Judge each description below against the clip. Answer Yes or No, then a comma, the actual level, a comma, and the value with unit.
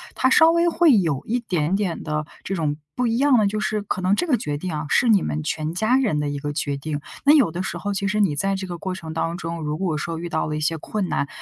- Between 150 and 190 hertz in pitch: Yes, medium, 185 Hz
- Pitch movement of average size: No, wide, 5.7 semitones